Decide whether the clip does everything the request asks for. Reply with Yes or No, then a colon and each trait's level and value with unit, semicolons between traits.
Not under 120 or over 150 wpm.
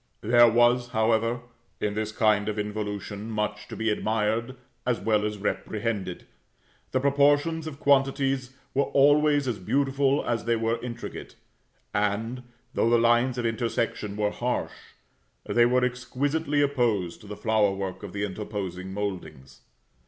Yes: average, 145 wpm